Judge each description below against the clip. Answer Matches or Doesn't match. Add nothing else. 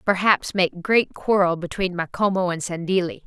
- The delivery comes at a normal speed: Matches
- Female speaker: Matches